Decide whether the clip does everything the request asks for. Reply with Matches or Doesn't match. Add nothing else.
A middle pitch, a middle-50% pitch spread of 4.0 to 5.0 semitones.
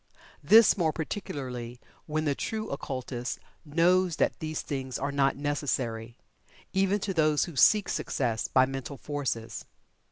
Matches